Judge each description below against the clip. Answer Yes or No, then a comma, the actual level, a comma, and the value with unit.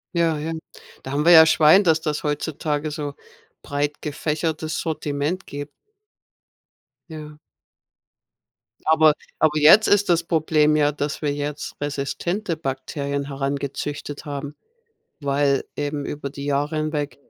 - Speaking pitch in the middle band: Yes, medium, 150 Hz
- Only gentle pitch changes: Yes, narrow, 1.7 semitones